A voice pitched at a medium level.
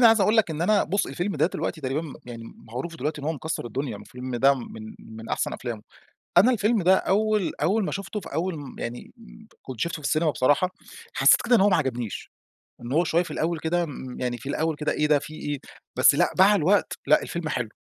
Yes: medium, 155 Hz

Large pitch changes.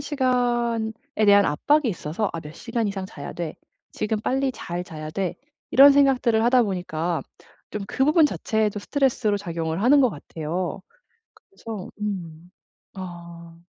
Yes: wide, 6.3 semitones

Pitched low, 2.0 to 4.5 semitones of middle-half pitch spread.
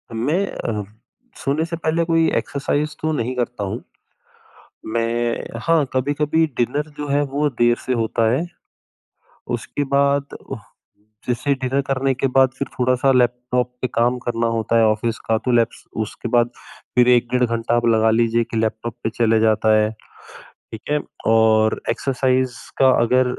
Yes: low, 125 Hz; average, 3.2 semitones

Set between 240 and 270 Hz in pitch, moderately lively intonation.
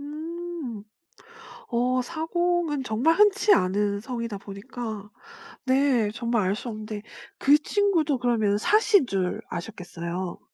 No: high, 245 Hz; wide, 7.2 semitones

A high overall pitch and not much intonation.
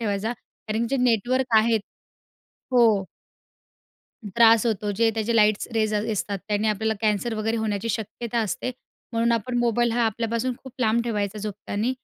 Yes: high, 225 Hz; narrow, 1.8 semitones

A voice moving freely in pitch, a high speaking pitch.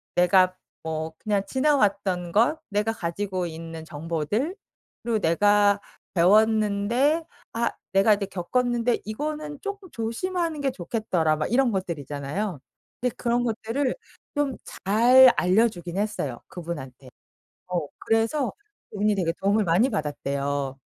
Yes: wide, 5.8 semitones; high, 205 Hz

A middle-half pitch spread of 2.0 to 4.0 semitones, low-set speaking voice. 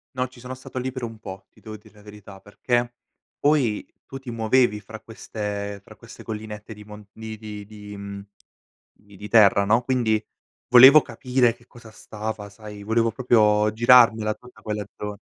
Yes: narrow, 2.5 semitones; low, 110 Hz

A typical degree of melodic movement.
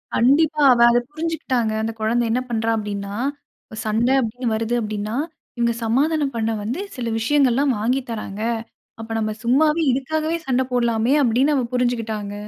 Yes: average, 3.5 semitones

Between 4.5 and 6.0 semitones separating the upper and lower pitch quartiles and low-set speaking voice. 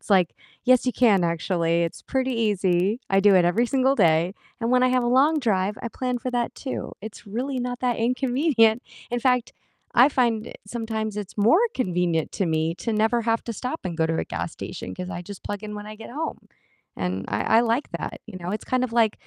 No: average, 5.1 semitones; high, 225 Hz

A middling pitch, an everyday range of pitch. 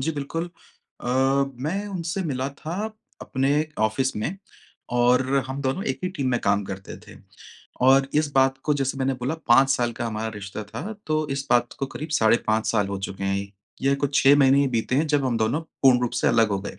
No: low, 130 Hz; average, 3.9 semitones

